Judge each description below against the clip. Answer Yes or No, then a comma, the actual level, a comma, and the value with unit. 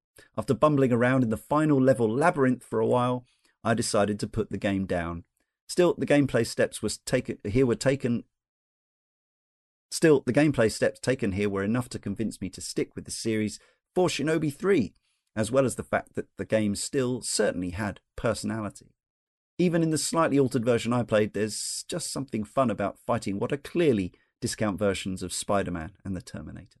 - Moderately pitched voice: No, low, 110 Hz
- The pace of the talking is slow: No, average, 185 wpm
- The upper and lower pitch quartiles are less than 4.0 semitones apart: No, average, 4.7 semitones